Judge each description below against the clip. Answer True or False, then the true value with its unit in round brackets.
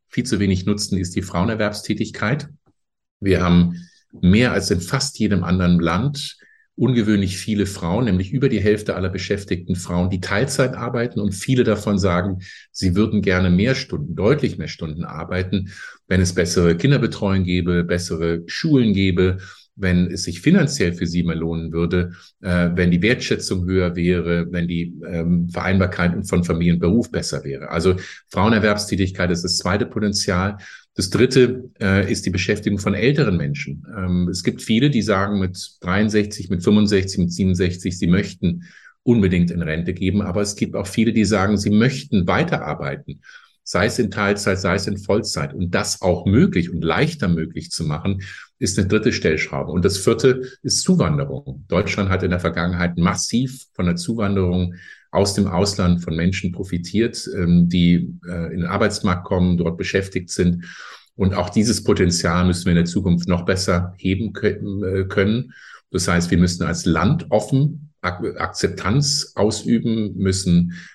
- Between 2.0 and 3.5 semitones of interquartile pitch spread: True (3.0 semitones)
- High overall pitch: False (95 Hz)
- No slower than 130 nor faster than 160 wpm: True (155 wpm)